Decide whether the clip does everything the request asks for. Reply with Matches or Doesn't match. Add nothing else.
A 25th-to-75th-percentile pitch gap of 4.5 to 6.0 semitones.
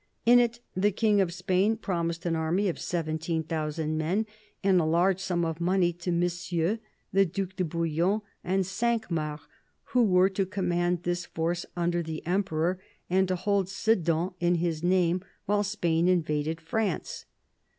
Doesn't match